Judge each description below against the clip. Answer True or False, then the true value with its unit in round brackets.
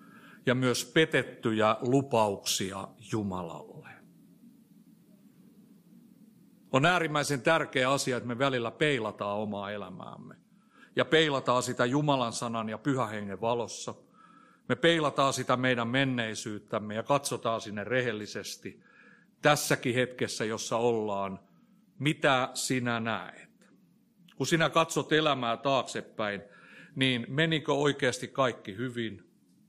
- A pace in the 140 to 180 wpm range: False (100 wpm)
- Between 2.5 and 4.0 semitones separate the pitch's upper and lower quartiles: False (5.3 semitones)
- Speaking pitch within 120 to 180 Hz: True (130 Hz)